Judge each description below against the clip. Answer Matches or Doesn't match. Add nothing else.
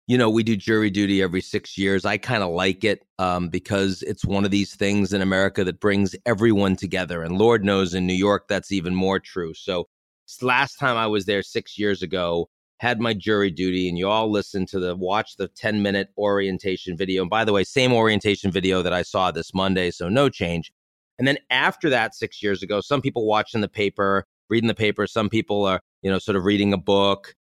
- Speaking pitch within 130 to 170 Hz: Doesn't match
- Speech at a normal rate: Doesn't match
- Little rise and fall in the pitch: Matches